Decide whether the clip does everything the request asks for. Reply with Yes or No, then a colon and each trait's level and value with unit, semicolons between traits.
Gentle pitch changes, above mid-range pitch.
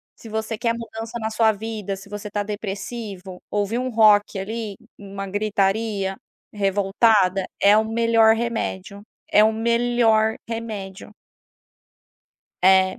Yes: narrow, 2.3 semitones; high, 215 Hz